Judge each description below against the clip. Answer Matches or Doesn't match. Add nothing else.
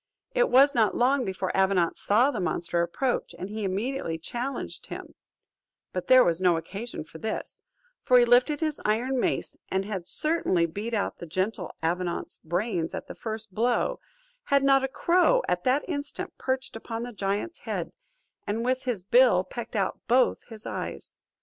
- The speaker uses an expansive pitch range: Matches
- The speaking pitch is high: Matches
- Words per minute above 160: Matches